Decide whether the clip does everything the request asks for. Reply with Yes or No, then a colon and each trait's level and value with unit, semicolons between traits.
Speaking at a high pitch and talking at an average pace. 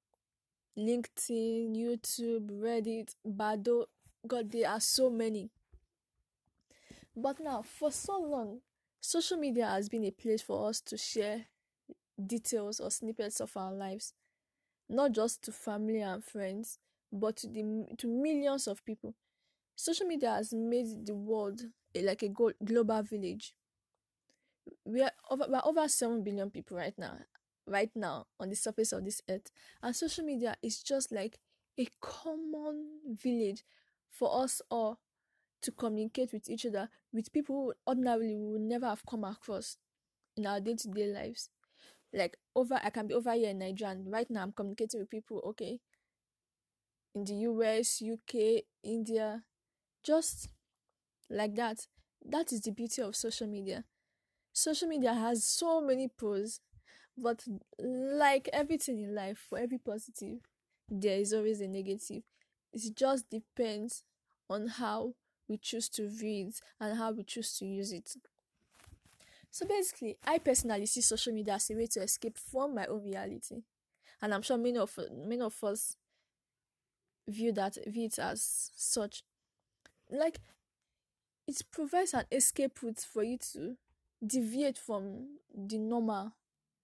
Yes: high, 225 Hz; average, 150 wpm